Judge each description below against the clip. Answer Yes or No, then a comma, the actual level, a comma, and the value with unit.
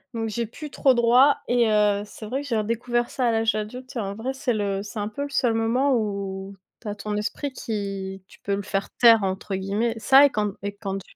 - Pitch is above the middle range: Yes, high, 220 Hz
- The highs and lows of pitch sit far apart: No, average, 3.2 semitones